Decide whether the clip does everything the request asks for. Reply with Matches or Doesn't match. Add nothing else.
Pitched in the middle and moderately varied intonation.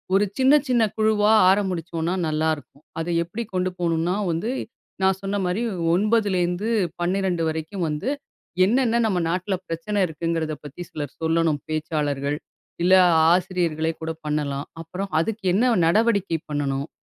Matches